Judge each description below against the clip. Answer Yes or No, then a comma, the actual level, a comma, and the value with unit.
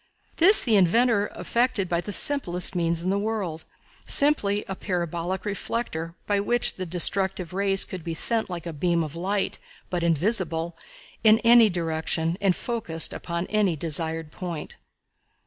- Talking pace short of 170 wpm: Yes, average, 150 wpm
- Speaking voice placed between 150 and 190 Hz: Yes, medium, 185 Hz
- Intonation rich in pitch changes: No, average, 3.7 semitones